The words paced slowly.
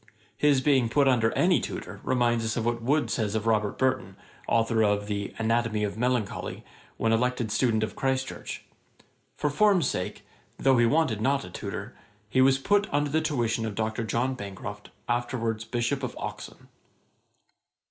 No: average, 170 wpm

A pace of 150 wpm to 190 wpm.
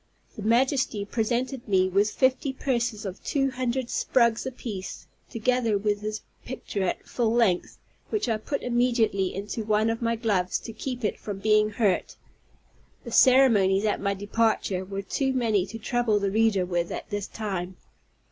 Yes: average, 165 wpm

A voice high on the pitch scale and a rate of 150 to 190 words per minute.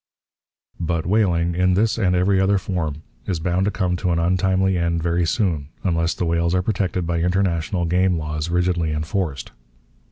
No: very low, 90 Hz; average, 170 wpm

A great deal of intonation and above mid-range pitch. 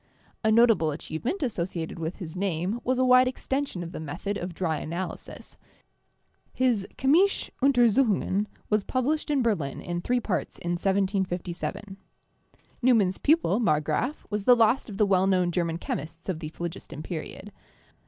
Yes: wide, 6.0 semitones; high, 195 Hz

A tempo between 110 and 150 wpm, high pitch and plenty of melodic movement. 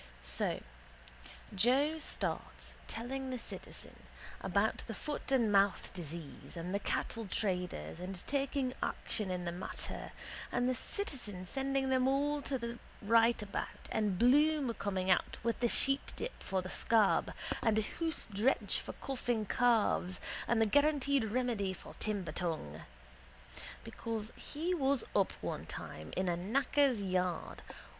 Yes: average, 140 wpm; high, 230 Hz; wide, 6.1 semitones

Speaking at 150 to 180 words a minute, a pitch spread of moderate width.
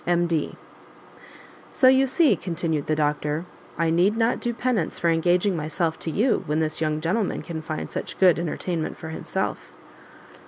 Yes: average, 160 wpm; average, 3.8 semitones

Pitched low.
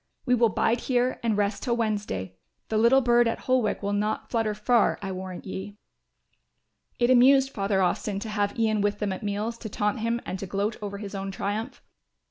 No: high, 215 Hz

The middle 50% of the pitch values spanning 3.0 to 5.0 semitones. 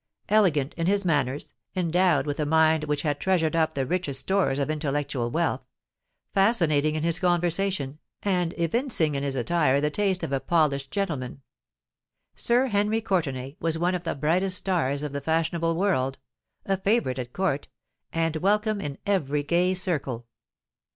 Yes: average, 4.7 semitones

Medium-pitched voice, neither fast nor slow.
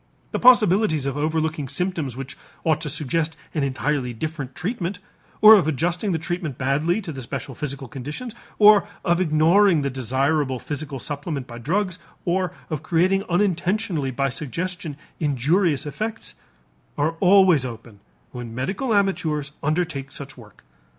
Yes: medium, 155 Hz; average, 145 wpm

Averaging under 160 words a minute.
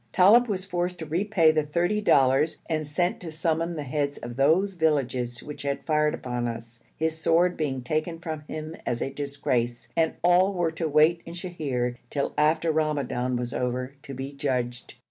No: average, 185 wpm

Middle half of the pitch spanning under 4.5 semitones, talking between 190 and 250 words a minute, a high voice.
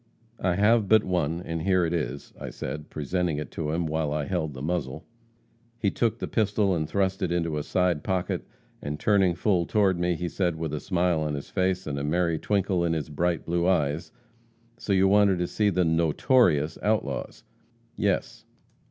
No: average, 3.5 semitones; average, 195 wpm; very low, 85 Hz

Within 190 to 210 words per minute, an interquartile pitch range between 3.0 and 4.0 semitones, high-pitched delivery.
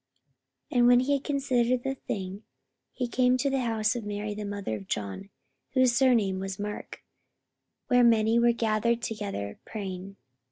No: average, 165 wpm; average, 3.6 semitones; high, 225 Hz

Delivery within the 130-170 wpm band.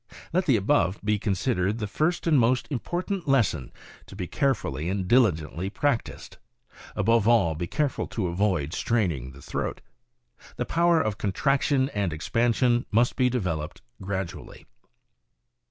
Yes: average, 140 wpm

